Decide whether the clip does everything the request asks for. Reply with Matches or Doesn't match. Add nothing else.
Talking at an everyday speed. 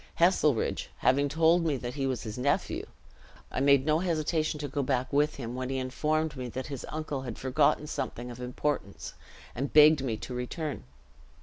Matches